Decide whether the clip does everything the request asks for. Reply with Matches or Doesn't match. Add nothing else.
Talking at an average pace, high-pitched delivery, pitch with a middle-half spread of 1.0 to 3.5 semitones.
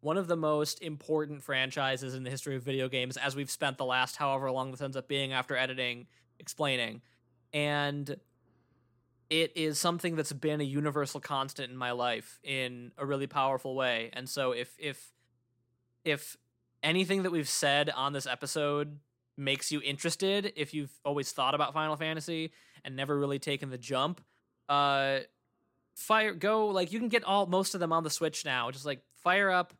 Doesn't match